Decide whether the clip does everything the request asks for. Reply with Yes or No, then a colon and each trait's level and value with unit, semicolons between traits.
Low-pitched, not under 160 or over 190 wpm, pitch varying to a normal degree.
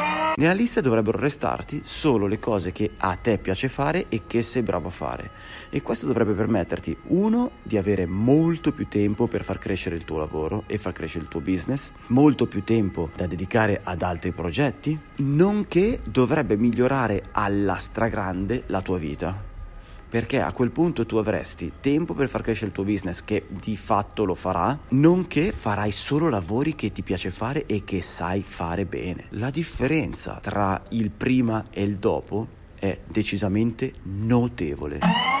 No: low, 105 Hz; average, 165 wpm; wide, 5.7 semitones